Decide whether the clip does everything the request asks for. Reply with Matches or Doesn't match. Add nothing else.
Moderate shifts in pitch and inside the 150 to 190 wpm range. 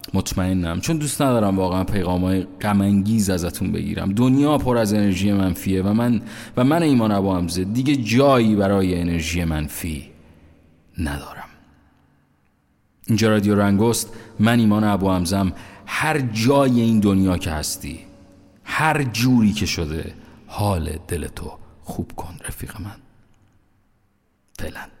Doesn't match